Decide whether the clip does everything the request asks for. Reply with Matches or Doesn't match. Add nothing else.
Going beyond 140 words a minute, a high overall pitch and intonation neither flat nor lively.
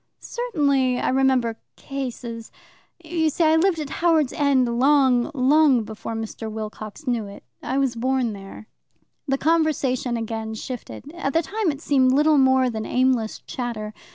Matches